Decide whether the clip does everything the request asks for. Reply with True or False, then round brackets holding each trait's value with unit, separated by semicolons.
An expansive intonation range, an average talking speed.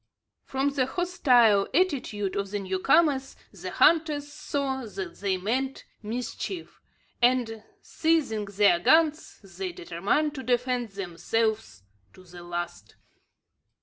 False (6.3 semitones; 115 wpm)